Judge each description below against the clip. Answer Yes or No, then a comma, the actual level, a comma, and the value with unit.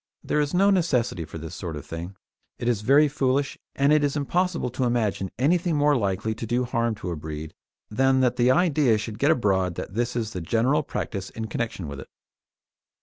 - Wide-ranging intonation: Yes, wide, 6.4 semitones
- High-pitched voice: No, low, 120 Hz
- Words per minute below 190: No, fast, 205 wpm